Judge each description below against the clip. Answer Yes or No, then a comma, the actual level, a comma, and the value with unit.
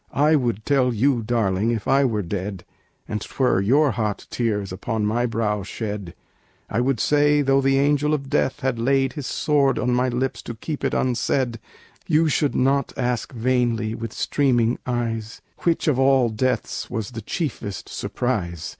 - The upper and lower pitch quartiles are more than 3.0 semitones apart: Yes, average, 3.7 semitones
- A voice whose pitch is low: Yes, low, 120 Hz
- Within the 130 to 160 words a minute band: No, average, 170 wpm